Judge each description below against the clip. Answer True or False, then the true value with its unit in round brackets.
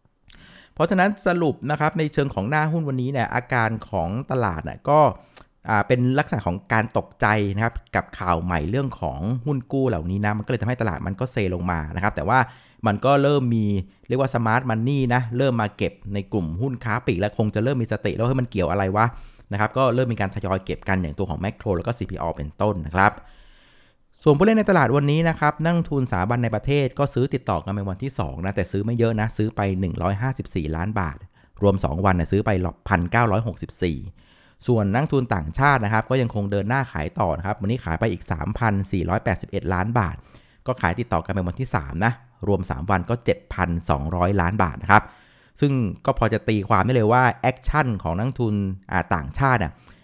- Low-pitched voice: True (105 Hz)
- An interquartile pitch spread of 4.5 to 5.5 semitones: True (5.1 semitones)